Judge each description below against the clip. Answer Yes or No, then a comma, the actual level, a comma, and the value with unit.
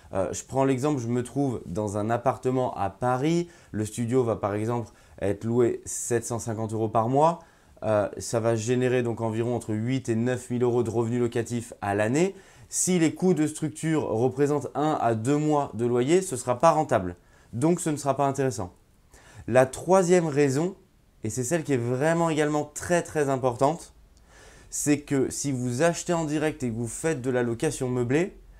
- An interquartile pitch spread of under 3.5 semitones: No, average, 4.7 semitones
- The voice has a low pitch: Yes, low, 130 Hz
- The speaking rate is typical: Yes, average, 190 wpm